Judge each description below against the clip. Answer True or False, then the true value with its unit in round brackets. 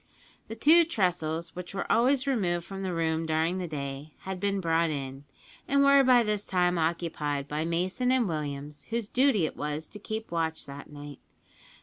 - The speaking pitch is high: False (175 Hz)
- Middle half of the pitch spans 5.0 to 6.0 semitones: True (5.6 semitones)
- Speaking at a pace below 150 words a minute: False (185 wpm)